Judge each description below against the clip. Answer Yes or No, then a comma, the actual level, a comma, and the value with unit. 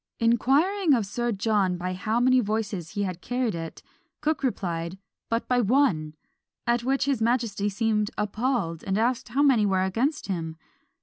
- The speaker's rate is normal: Yes, average, 165 wpm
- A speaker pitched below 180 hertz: No, high, 220 Hz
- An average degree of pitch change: Yes, average, 4.8 semitones